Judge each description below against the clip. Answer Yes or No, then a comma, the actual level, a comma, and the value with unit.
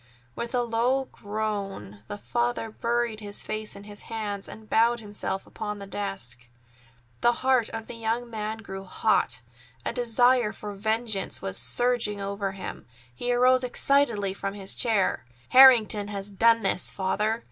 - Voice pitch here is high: Yes, high, 215 Hz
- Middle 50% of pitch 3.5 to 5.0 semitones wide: No, average, 3.0 semitones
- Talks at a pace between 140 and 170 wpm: Yes, average, 160 wpm